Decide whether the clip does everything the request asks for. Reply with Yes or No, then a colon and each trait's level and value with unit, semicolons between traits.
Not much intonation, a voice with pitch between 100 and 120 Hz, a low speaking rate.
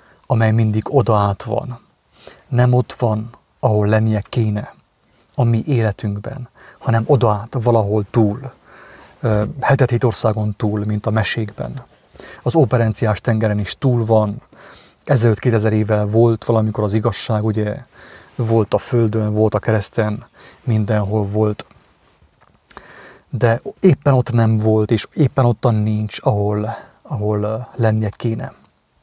Yes: narrow, 2.2 semitones; low, 110 Hz; slow, 125 wpm